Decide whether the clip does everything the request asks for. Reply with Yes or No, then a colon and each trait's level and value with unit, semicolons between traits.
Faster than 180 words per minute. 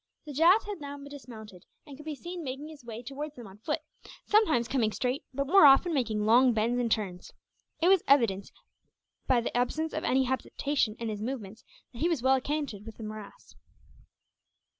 Yes: average, 190 wpm